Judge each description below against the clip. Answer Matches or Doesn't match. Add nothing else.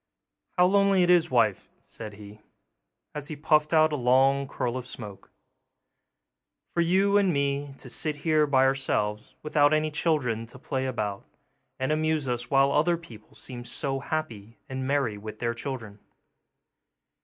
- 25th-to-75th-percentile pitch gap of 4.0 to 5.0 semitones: Matches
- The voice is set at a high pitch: Doesn't match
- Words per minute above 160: Doesn't match